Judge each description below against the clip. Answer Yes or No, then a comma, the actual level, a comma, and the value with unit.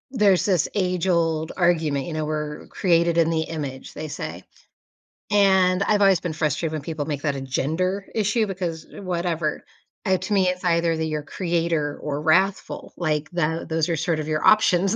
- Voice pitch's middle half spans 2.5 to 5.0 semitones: Yes, average, 3.0 semitones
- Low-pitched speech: No, medium, 165 Hz